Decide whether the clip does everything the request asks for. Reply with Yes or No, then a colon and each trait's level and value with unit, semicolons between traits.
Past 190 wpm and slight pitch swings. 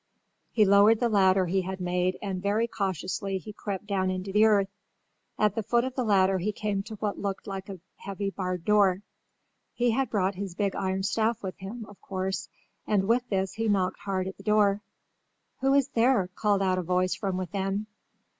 Yes: average, 200 wpm; narrow, 2.1 semitones